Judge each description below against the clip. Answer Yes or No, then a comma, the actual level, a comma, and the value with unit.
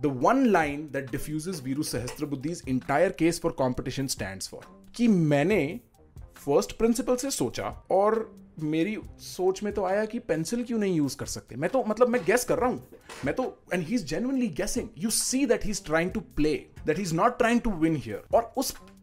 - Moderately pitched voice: Yes, medium, 180 Hz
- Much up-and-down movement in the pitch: Yes, wide, 7.4 semitones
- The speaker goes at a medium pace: Yes, average, 195 wpm